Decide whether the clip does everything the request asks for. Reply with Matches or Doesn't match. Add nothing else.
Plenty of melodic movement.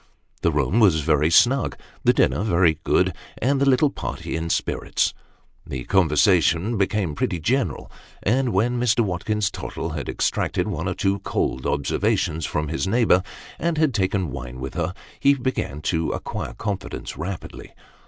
Matches